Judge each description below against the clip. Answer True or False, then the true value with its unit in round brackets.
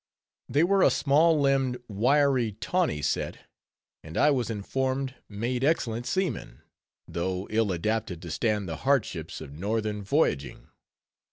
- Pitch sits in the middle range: False (115 Hz)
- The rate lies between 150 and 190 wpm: False (135 wpm)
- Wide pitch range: True (5.9 semitones)